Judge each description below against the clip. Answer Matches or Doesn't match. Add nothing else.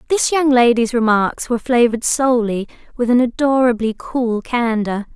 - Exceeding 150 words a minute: Doesn't match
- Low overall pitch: Doesn't match